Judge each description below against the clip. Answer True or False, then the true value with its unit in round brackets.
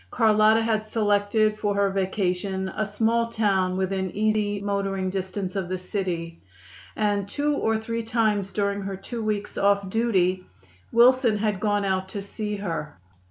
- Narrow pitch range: True (2.2 semitones)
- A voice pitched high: True (205 Hz)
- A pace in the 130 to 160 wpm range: True (155 wpm)